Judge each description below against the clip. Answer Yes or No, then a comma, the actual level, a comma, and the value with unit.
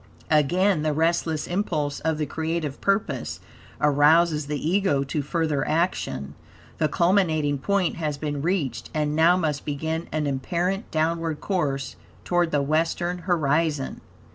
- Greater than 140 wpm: No, slow, 135 wpm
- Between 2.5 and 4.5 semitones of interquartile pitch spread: Yes, average, 2.8 semitones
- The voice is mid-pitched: Yes, medium, 155 Hz